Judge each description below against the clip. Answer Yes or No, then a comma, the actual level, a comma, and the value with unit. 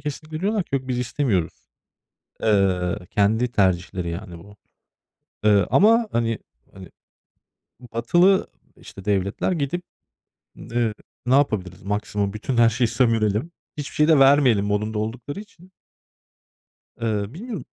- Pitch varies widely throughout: Yes, wide, 5.9 semitones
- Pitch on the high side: No, low, 115 Hz